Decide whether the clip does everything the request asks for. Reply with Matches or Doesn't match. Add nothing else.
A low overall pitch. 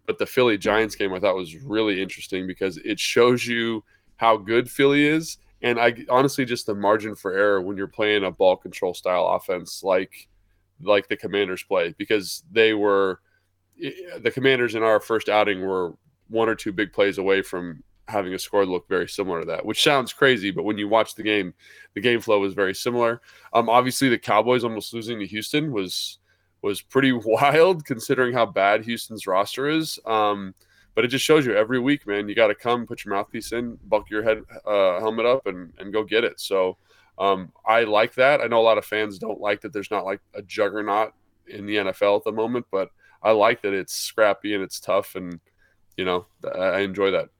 Matches